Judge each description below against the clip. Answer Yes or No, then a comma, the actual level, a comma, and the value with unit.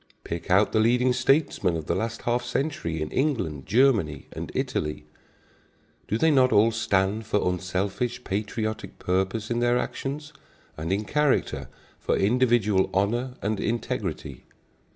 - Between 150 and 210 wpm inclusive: No, average, 140 wpm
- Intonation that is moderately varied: Yes, average, 4.7 semitones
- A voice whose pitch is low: Yes, low, 110 Hz